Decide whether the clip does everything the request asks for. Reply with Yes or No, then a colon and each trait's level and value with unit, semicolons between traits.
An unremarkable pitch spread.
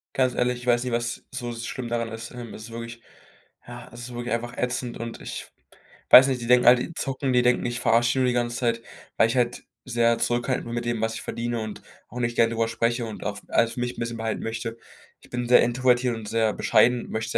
No: narrow, 1.0 semitones